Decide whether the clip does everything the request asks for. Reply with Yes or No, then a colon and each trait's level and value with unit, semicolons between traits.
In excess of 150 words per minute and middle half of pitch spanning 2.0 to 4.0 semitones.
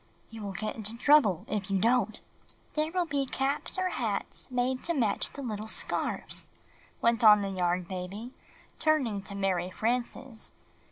No: average, 160 wpm; average, 4.9 semitones